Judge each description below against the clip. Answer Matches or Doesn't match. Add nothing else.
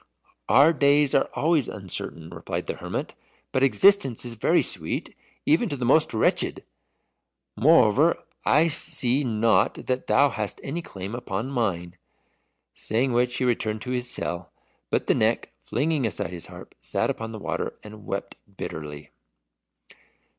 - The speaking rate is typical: Matches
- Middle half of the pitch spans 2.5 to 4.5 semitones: Doesn't match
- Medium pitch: Doesn't match